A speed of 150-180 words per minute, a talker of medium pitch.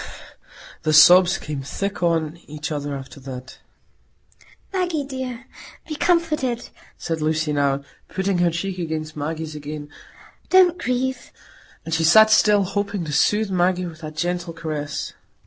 No: average, 140 wpm; medium, 170 Hz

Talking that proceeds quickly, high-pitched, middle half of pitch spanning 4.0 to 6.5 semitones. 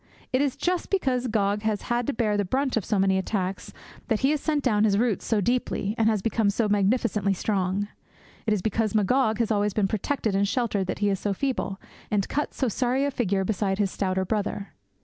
No: fast, 220 wpm; high, 215 Hz; average, 3.6 semitones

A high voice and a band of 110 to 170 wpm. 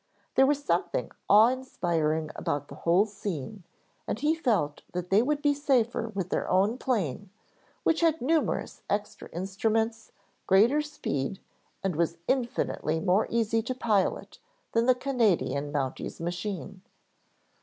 Yes: high, 210 Hz; slow, 135 wpm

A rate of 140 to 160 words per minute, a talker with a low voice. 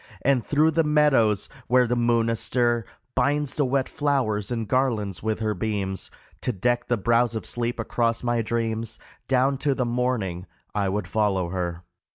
No: average, 195 wpm; low, 115 Hz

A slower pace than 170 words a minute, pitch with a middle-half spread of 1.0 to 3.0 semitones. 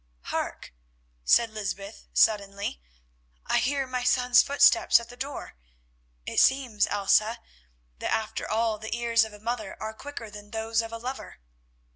Yes: average, 150 wpm; narrow, 2.6 semitones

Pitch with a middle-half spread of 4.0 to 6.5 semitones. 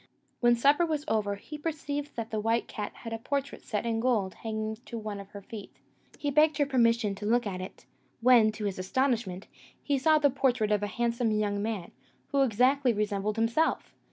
Yes: average, 4.4 semitones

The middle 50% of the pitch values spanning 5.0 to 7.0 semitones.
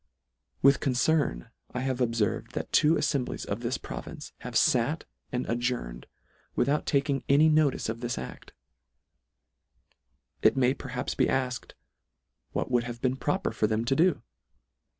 No: average, 2.9 semitones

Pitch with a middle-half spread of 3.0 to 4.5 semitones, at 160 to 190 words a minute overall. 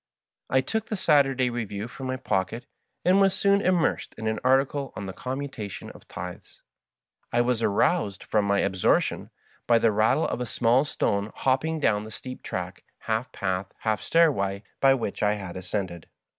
No: average, 5.0 semitones; average, 180 wpm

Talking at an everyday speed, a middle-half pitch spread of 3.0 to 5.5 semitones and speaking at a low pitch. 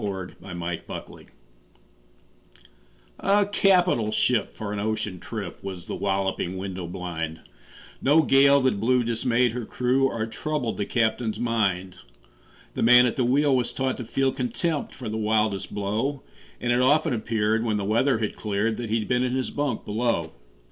Yes: average, 170 wpm; average, 4.1 semitones; low, 115 Hz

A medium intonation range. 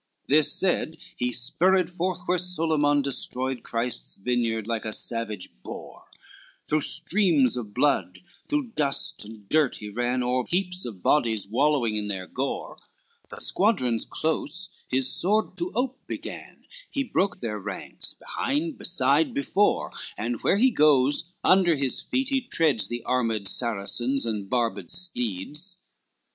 No: wide, 7.6 semitones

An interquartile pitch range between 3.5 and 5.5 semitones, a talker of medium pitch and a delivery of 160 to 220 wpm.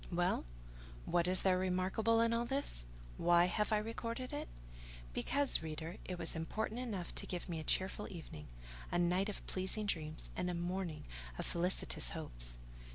Yes: average, 3.9 semitones; medium, 180 Hz; average, 165 wpm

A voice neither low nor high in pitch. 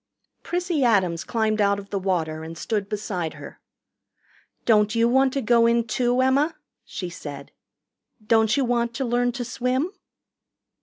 No: high, 230 Hz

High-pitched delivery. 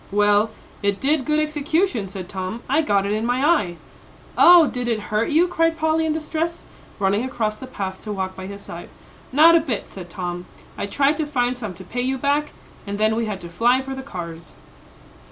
Yes: high, 240 Hz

